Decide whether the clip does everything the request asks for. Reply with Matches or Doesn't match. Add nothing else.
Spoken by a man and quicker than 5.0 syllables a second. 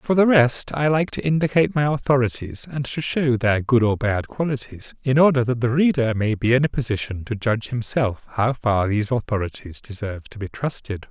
Matches